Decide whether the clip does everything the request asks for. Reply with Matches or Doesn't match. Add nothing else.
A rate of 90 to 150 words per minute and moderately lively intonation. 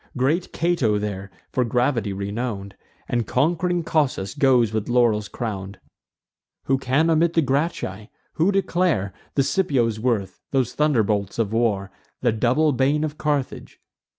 Doesn't match